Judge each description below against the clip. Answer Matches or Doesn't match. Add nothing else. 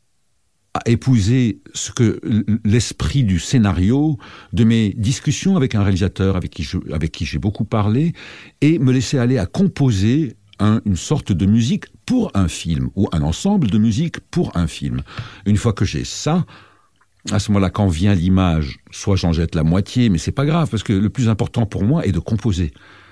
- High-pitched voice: Doesn't match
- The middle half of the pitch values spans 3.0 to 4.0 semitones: Doesn't match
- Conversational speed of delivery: Matches